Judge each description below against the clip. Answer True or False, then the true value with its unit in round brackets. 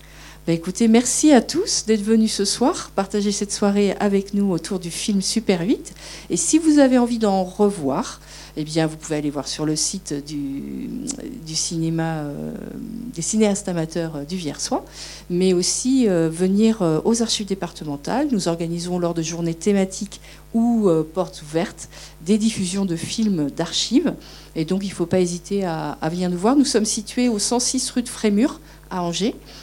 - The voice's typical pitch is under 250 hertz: True (190 Hz)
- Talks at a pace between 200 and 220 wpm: False (180 wpm)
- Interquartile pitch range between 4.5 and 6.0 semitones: True (5.2 semitones)